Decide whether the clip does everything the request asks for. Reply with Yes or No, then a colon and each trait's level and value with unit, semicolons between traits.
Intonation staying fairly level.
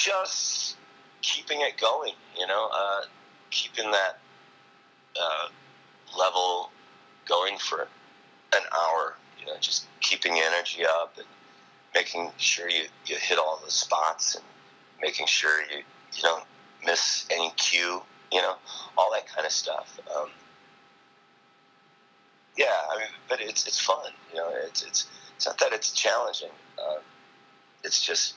Yes: narrow, 1.0 semitones